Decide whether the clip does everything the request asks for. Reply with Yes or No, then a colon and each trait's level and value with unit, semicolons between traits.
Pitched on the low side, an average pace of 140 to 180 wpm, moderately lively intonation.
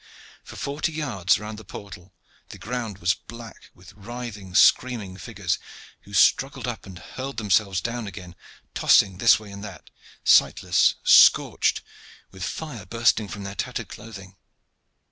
Yes: low, 105 Hz; average, 145 wpm; average, 3.6 semitones